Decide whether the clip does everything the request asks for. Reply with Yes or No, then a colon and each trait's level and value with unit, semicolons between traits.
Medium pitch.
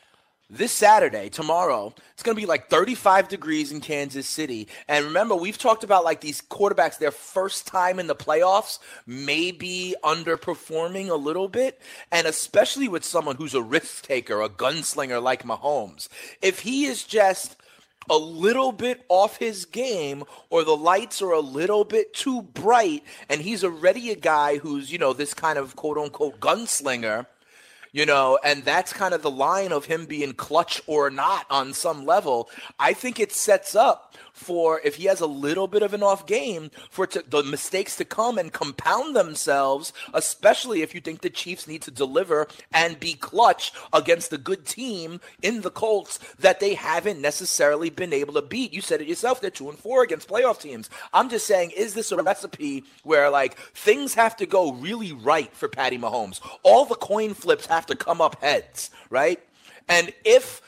Yes: medium, 180 Hz